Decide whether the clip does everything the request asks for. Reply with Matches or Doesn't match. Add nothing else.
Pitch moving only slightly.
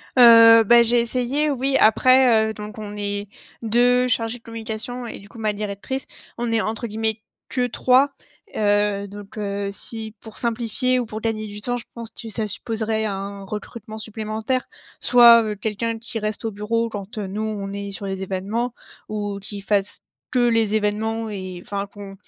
Matches